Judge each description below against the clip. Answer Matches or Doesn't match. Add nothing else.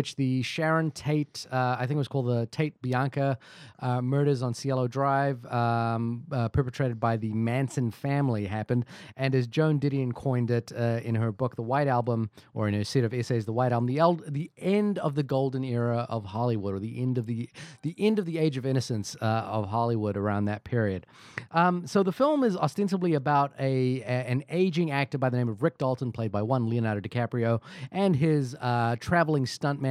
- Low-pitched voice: Matches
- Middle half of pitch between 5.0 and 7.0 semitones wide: Doesn't match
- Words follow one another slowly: Doesn't match